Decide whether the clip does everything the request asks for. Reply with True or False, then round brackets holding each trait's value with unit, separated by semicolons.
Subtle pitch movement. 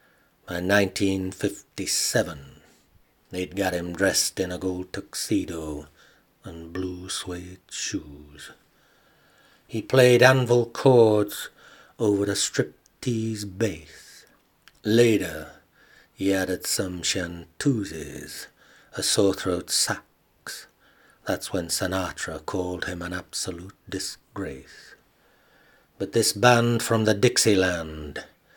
False (3.9 semitones)